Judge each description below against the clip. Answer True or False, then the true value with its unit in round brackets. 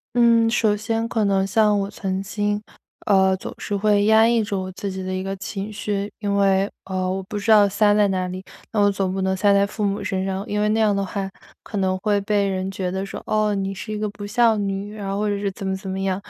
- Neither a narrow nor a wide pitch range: False (1.6 semitones)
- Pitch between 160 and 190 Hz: False (200 Hz)